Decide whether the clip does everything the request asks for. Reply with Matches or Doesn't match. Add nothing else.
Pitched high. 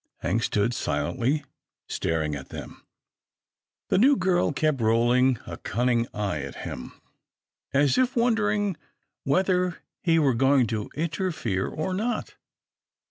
Doesn't match